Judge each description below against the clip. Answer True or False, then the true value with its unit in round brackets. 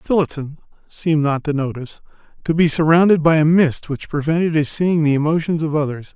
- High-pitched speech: False (155 Hz)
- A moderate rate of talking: True (185 wpm)